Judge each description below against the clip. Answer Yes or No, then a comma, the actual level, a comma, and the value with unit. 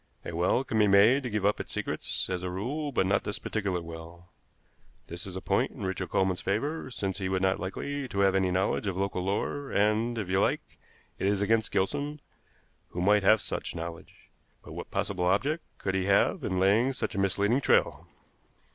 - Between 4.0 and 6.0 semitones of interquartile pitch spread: No, average, 3.1 semitones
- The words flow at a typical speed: No, fast, 210 wpm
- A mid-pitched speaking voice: No, low, 100 Hz